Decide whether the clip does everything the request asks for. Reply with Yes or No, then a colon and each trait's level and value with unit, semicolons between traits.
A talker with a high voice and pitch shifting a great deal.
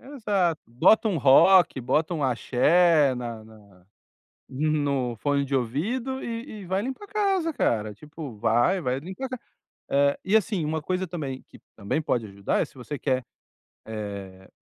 No: medium, 150 Hz; wide, 7.5 semitones